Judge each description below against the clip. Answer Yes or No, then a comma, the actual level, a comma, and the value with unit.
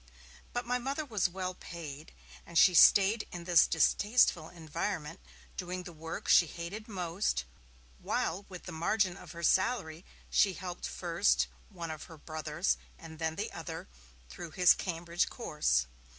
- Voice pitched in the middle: Yes, medium, 175 Hz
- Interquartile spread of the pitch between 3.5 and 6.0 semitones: No, average, 3.1 semitones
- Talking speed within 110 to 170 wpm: Yes, average, 150 wpm